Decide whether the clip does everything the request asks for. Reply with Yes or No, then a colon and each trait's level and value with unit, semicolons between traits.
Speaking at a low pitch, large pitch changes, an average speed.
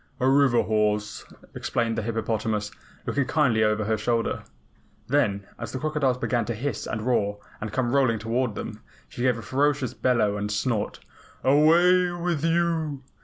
No: low, 120 Hz; average, 4.6 semitones; average, 160 wpm